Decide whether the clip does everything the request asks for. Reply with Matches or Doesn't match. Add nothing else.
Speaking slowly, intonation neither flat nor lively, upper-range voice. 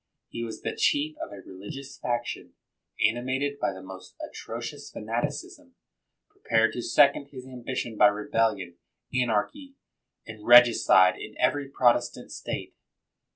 Doesn't match